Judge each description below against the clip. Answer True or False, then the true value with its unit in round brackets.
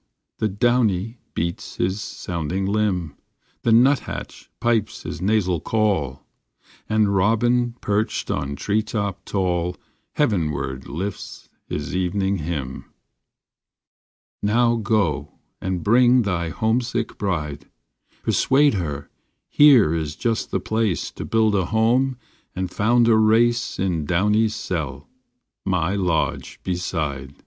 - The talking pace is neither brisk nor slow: False (115 wpm)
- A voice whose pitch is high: False (100 Hz)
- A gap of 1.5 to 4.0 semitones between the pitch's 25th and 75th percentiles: False (4.8 semitones)